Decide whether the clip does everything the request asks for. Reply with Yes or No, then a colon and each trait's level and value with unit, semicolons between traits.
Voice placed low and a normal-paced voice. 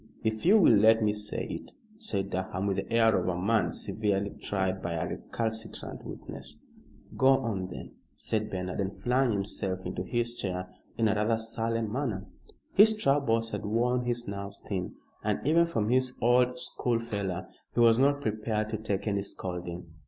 Yes: low, 110 Hz; average, 175 wpm